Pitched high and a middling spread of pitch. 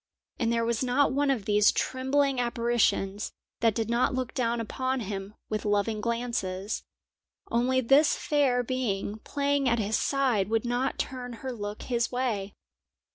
Yes: high, 235 Hz; average, 3.3 semitones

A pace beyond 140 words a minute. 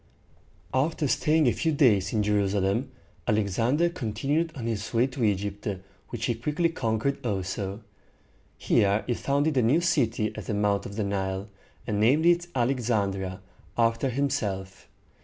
Yes: average, 160 wpm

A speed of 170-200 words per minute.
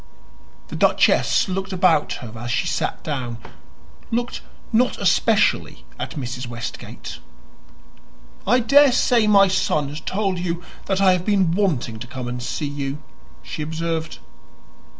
No: slow, 135 wpm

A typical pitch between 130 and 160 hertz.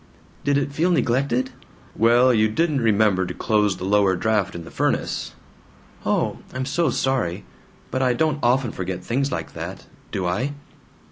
No: low, 120 Hz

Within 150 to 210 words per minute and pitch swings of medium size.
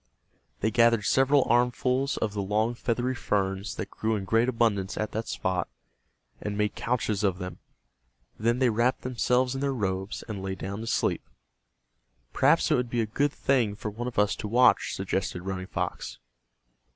Yes: average, 175 wpm; average, 3.5 semitones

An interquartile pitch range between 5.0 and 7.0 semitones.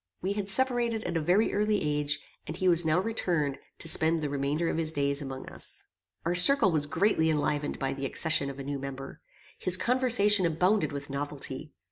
Yes: average, 5.3 semitones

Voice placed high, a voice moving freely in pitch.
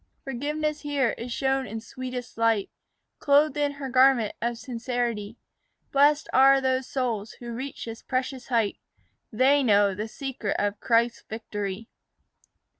No: very high, 250 Hz; average, 3.2 semitones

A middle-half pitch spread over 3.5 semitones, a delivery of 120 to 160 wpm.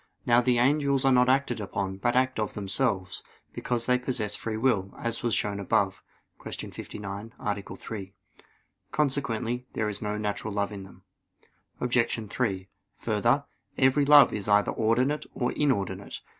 Yes: average, 3.9 semitones; average, 155 wpm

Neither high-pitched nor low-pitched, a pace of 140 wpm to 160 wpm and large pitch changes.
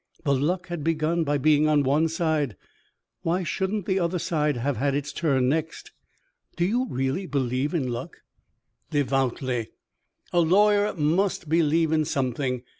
No: medium, 155 Hz; average, 150 wpm; average, 3.9 semitones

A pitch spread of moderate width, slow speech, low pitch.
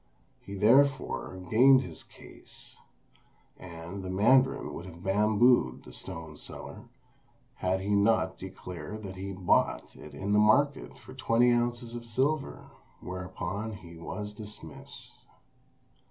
Yes: average, 4.4 semitones; slow, 125 wpm; low, 105 Hz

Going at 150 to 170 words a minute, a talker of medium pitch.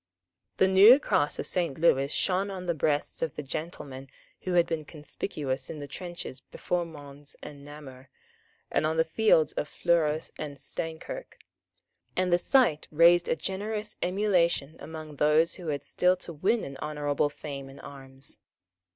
Yes: average, 160 wpm; medium, 160 Hz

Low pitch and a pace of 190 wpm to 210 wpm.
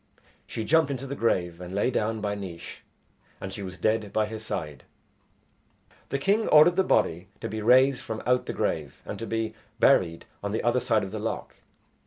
Yes: low, 110 Hz; average, 200 wpm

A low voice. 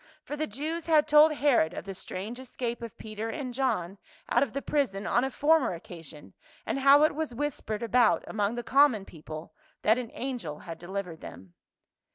No: high, 240 Hz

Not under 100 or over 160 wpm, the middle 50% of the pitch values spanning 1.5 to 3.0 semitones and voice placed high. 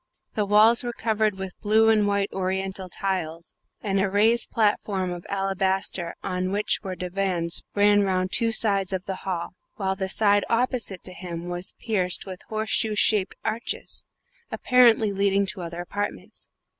Yes: average, 155 wpm; narrow, 2.4 semitones; high, 195 Hz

